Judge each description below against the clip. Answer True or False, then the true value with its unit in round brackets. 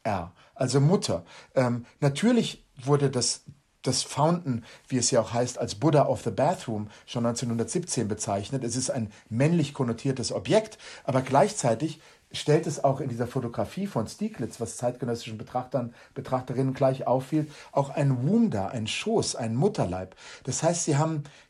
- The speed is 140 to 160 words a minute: True (150 wpm)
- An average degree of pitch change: True (4.0 semitones)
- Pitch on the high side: False (135 Hz)